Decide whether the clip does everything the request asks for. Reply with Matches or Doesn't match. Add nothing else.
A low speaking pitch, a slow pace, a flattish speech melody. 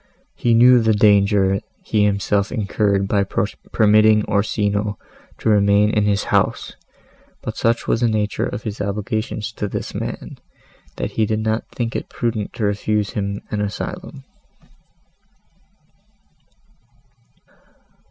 Matches